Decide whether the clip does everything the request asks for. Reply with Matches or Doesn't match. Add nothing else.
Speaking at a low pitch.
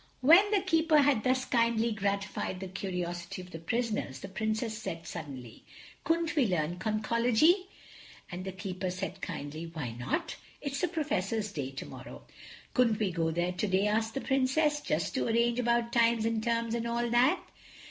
Doesn't match